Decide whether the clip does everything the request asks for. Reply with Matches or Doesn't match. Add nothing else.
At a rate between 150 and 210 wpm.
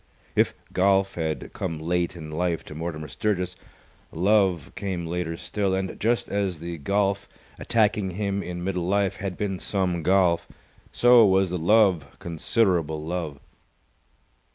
Doesn't match